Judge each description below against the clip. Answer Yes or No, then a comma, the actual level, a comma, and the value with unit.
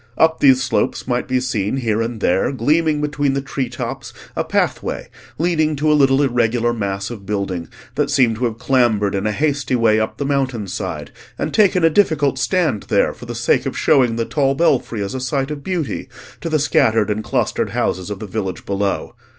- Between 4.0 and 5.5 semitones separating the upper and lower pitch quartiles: Yes, average, 4.9 semitones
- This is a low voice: Yes, low, 125 Hz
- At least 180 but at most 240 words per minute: Yes, fast, 205 wpm